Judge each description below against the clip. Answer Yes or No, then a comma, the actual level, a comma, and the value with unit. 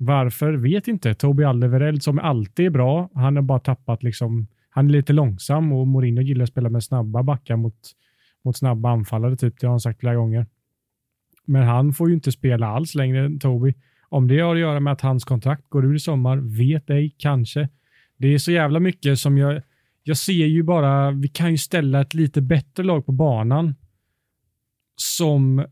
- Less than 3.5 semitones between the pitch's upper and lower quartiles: Yes, average, 3.1 semitones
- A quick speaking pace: Yes, fast, 200 wpm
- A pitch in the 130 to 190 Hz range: Yes, low, 135 Hz